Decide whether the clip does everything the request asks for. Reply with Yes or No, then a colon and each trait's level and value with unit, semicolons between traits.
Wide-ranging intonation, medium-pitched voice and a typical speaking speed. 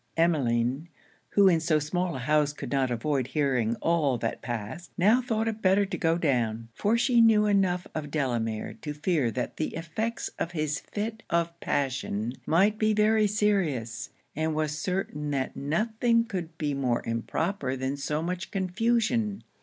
Yes: wide, 6.9 semitones; medium, 160 Hz; average, 165 wpm